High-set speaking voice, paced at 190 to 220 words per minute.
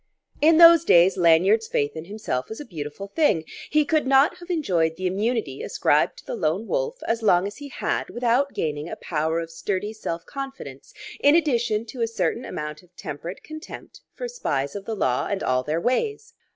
Yes: high, 210 Hz; average, 195 wpm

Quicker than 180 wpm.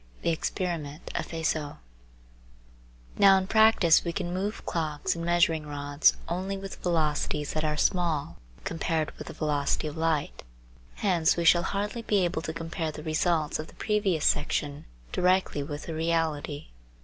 No: average, 155 wpm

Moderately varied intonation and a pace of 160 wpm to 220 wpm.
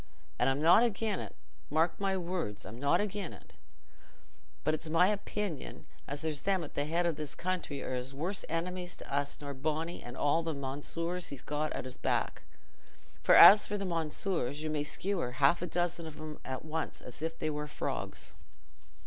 Yes: average, 3.8 semitones; average, 190 wpm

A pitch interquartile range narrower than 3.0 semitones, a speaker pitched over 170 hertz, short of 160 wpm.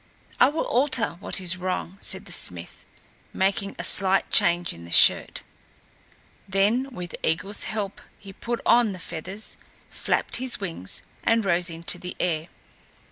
No: average, 3.7 semitones; high, 190 Hz; average, 150 wpm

